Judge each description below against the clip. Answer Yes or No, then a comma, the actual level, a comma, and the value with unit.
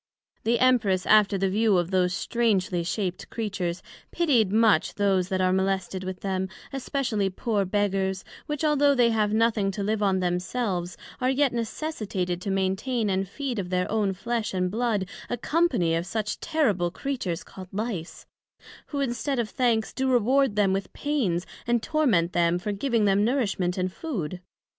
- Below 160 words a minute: No, average, 165 wpm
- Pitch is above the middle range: Yes, high, 205 Hz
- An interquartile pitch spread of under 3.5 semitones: No, average, 4.4 semitones